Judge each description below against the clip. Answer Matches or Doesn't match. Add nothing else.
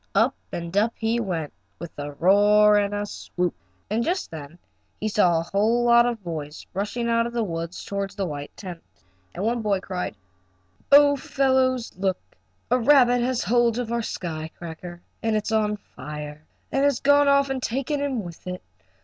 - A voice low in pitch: Doesn't match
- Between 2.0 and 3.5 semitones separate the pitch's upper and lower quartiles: Doesn't match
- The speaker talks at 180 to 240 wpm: Matches